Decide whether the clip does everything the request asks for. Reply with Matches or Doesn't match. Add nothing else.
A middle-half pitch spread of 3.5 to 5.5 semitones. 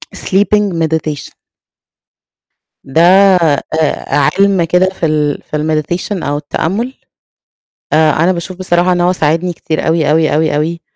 Doesn't match